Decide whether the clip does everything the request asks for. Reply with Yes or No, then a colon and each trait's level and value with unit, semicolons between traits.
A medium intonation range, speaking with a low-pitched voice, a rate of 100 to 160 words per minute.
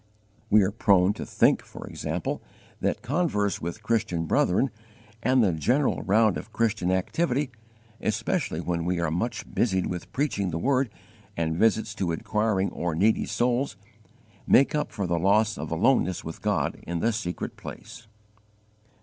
Yes: average, 4.7 semitones; low, 105 Hz; average, 155 wpm